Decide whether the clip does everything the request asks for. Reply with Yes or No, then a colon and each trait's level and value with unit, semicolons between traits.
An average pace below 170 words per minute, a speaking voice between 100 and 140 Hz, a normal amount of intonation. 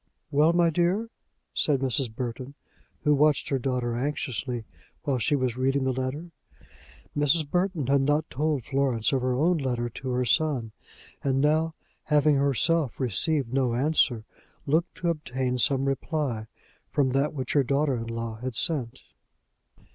Yes: average, 155 wpm; low, 135 Hz; average, 3.2 semitones